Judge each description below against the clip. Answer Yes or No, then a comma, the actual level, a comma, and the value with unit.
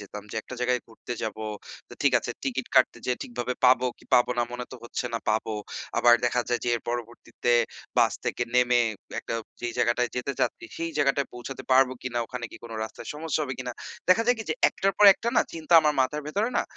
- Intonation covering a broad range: No, average, 2.7 semitones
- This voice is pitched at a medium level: No, low, 125 Hz